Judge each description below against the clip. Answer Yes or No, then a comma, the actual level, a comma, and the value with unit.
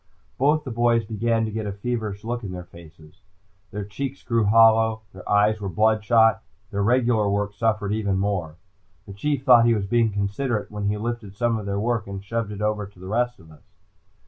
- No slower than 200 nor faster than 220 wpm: Yes, fast, 205 wpm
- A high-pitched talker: No, low, 110 Hz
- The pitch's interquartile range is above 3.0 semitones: No, narrow, 2.6 semitones